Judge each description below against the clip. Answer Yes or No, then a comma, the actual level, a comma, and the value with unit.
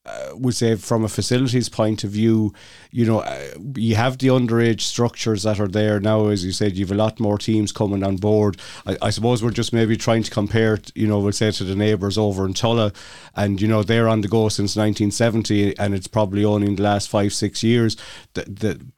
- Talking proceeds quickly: Yes, fast, 230 wpm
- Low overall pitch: Yes, low, 110 Hz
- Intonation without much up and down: Yes, narrow, 1.8 semitones